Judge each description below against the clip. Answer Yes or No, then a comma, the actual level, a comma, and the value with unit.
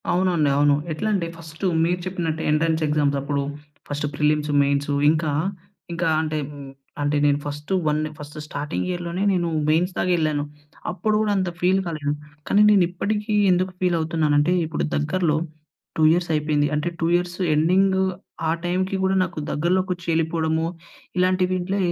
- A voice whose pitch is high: No, medium, 165 Hz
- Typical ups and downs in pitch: Yes, average, 3.3 semitones